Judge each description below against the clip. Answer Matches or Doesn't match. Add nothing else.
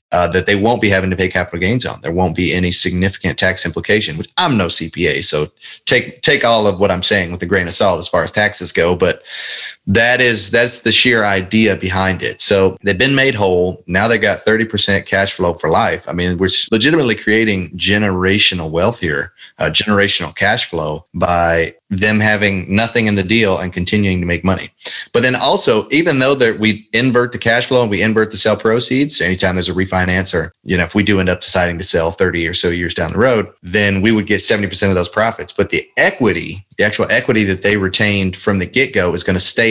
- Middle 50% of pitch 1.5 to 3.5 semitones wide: Matches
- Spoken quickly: Matches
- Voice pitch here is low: Matches